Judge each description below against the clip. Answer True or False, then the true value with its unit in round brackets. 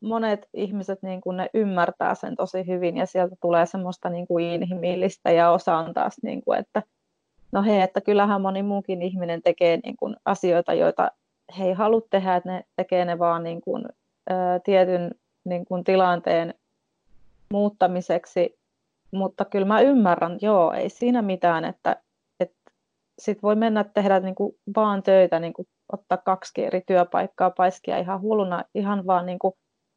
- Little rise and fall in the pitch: True (2.2 semitones)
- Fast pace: True (160 wpm)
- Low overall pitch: False (185 Hz)